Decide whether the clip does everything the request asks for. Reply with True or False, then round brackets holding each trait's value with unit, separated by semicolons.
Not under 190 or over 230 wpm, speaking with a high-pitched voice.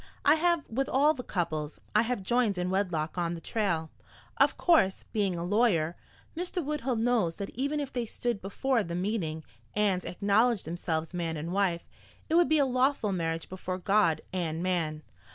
False (180 wpm; 195 Hz)